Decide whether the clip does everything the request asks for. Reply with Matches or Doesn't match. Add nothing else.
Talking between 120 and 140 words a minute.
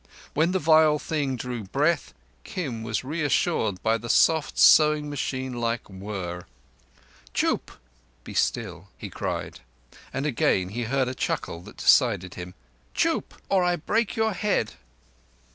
Matches